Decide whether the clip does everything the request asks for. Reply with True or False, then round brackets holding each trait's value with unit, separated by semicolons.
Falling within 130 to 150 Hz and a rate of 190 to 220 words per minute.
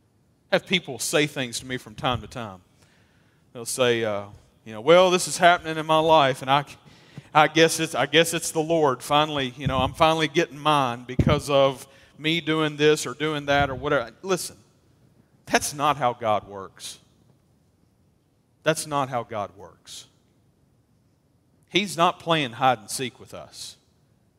False (140 Hz; 165 wpm)